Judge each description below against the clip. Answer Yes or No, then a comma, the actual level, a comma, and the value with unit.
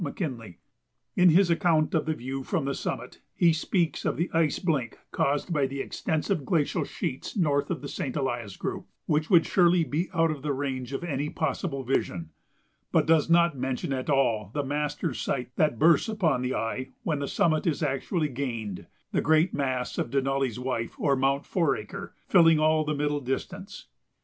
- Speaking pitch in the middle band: Yes, medium, 145 Hz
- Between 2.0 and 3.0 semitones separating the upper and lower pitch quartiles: No, average, 3.7 semitones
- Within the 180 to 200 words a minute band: Yes, average, 185 wpm